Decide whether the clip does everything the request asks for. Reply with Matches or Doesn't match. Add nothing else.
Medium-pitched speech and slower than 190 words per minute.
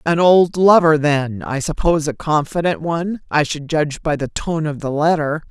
Doesn't match